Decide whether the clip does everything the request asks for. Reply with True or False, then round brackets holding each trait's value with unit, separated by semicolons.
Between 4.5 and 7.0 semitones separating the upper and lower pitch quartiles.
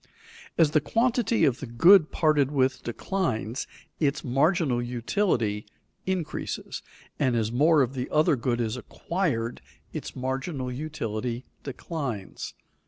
True (5.0 semitones)